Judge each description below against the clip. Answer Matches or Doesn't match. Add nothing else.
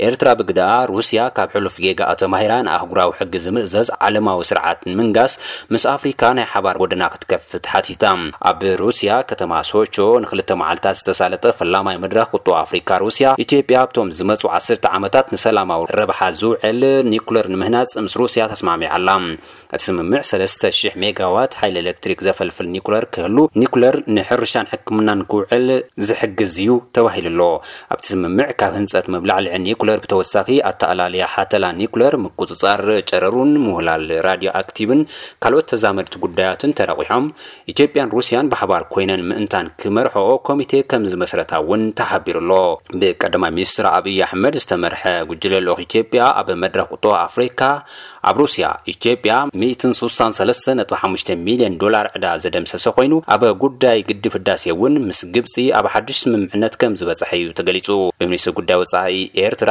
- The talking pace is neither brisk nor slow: Doesn't match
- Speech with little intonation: Doesn't match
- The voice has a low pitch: Matches